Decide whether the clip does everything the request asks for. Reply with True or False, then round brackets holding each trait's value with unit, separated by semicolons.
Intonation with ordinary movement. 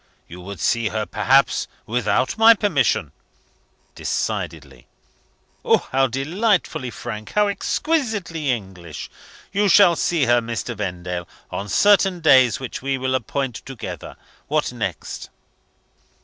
False (8.4 semitones)